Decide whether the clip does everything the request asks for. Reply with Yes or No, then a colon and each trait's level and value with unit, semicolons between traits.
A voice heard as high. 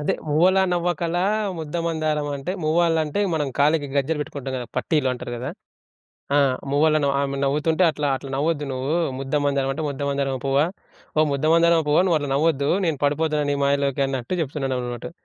No: medium, 145 Hz